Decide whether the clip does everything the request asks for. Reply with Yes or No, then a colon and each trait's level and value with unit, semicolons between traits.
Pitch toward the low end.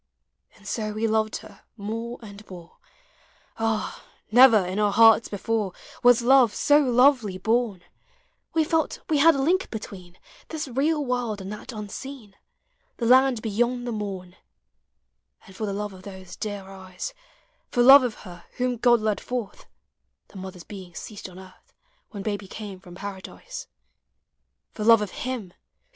No: high, 215 Hz